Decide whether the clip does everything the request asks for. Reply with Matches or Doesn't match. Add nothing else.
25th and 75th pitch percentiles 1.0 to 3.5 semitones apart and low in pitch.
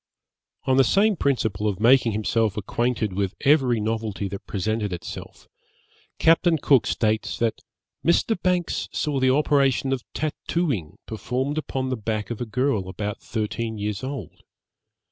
Doesn't match